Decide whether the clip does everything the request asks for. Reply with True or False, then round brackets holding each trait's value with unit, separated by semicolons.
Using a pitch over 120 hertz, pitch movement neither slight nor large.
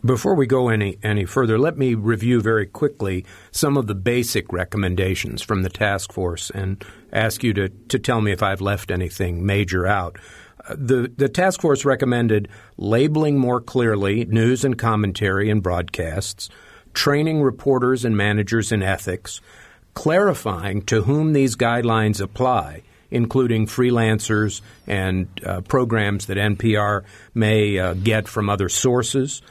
False (110 Hz; 3.9 semitones)